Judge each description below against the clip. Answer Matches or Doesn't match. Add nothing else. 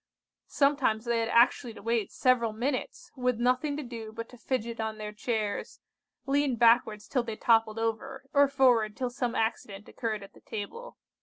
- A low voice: Doesn't match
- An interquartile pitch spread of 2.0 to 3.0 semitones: Matches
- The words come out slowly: Doesn't match